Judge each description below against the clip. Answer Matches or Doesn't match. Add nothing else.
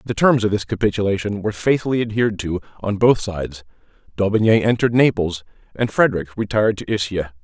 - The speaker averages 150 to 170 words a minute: Matches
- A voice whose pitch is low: Matches